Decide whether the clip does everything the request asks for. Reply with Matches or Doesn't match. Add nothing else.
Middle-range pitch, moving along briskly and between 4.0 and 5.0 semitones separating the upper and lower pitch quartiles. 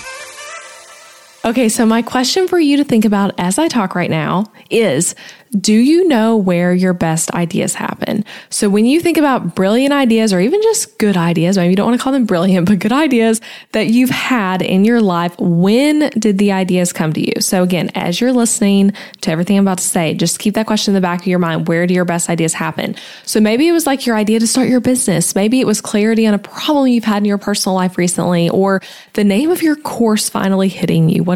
Doesn't match